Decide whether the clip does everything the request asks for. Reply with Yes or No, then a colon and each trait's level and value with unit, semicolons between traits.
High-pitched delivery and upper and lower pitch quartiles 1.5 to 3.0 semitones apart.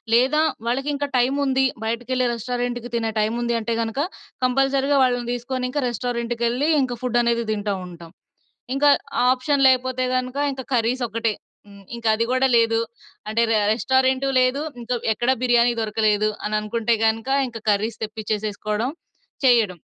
Yes: high, 240 Hz; narrow, 2.5 semitones